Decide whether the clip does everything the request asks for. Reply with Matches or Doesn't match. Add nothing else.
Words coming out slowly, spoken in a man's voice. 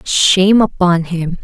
Doesn't match